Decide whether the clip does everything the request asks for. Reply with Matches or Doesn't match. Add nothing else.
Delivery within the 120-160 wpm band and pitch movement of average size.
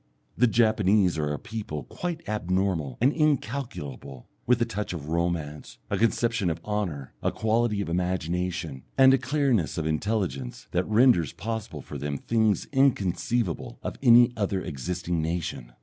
Doesn't match